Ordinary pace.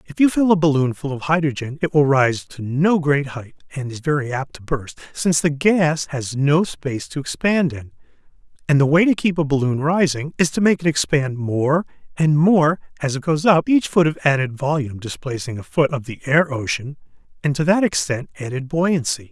No: fast, 210 wpm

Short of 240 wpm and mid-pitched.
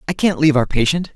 No: fast, 260 wpm; medium, 150 Hz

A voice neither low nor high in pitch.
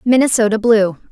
No: high, 225 Hz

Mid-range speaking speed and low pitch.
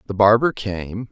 Yes: average, 160 wpm; low, 105 Hz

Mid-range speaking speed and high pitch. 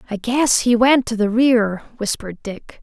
Yes: average, 190 wpm; high, 230 Hz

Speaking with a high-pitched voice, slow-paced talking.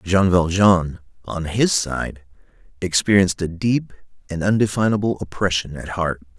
No: very low, 90 Hz; slow, 120 wpm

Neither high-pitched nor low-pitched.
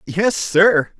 Yes: medium, 180 Hz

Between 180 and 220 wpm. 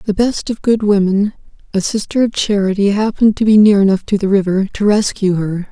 Yes: average, 190 wpm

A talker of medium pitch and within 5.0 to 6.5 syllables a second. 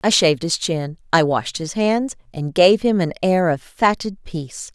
No: medium, 175 Hz; 4.5 syllables/s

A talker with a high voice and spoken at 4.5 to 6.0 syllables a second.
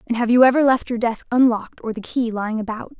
No: high, 235 Hz; 6.6 syllables/s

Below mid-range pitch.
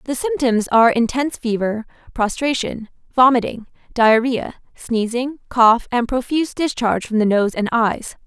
No: high, 240 Hz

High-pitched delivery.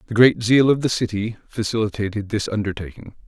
No: low, 110 Hz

